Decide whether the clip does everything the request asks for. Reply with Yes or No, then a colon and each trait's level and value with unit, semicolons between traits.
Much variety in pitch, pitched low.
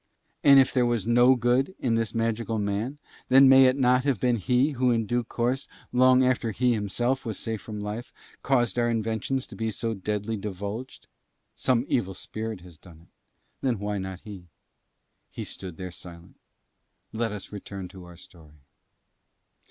No: average, 3.8 semitones; low, 115 Hz